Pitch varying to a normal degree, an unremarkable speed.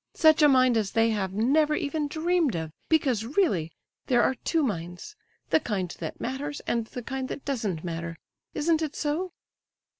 No: wide, 6.9 semitones; average, 170 wpm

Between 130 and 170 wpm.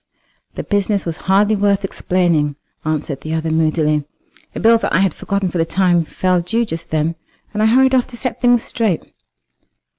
No: average, 185 wpm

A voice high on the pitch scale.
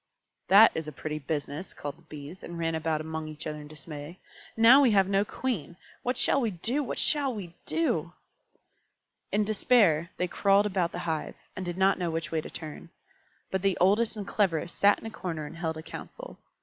No: medium, 175 Hz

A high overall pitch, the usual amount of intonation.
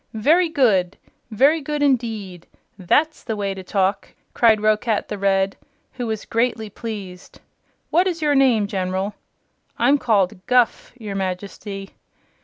Yes: high, 215 Hz; average, 4.6 semitones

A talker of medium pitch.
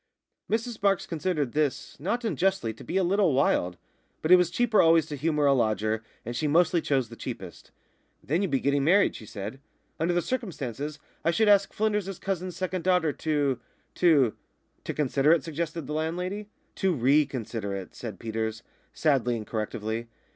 Yes: medium, 155 Hz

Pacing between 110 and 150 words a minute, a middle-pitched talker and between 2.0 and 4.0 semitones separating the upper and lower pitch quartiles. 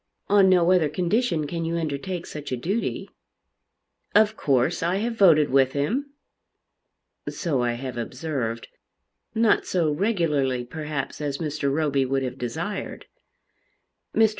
No: slow, 135 wpm; medium, 155 Hz; average, 5.3 semitones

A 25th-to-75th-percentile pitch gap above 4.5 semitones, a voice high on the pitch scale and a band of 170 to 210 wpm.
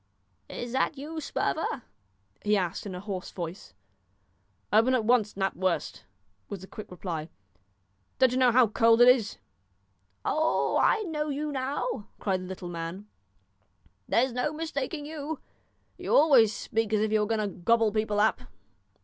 No: average, 5.1 semitones; high, 225 Hz; average, 160 wpm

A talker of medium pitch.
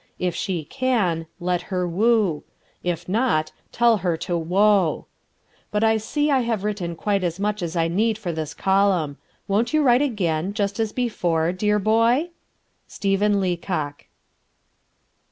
No: high, 195 Hz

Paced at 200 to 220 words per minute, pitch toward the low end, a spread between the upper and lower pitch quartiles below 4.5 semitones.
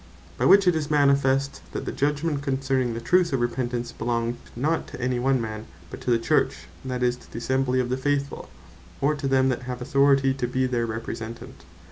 Yes: fast, 205 wpm; low, 130 Hz; narrow, 2.5 semitones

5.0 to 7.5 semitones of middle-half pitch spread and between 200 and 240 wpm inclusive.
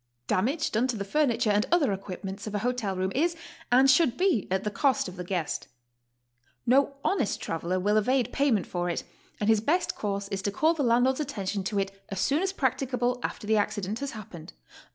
Yes: wide, 5.4 semitones; fast, 205 wpm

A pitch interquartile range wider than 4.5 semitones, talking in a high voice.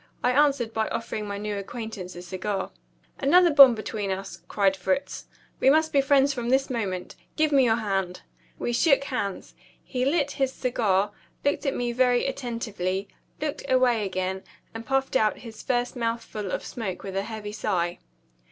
Yes: average, 5.2 semitones; high, 230 Hz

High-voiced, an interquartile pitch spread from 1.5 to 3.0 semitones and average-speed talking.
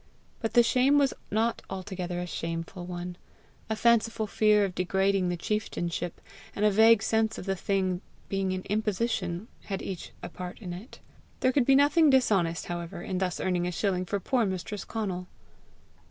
No: high, 195 Hz; average, 3.6 semitones; average, 175 wpm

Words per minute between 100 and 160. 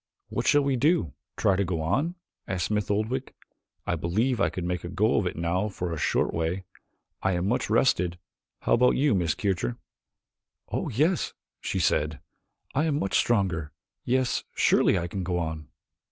No: average, 180 wpm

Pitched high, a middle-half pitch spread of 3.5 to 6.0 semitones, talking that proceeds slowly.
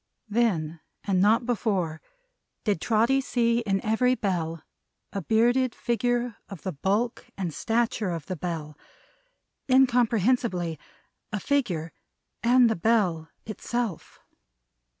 Yes: high, 215 Hz; average, 5.1 semitones; slow, 110 wpm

